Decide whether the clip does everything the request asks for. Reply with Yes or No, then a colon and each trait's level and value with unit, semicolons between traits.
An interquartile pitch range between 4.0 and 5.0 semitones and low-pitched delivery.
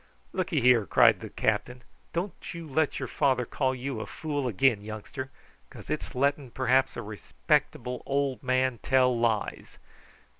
No: narrow, 2.6 semitones; low, 130 Hz